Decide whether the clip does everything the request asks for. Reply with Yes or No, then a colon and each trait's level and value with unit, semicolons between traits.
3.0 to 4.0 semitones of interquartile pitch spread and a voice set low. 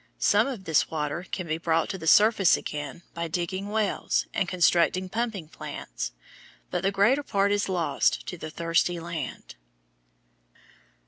No: average, 3.3 semitones; medium, 175 Hz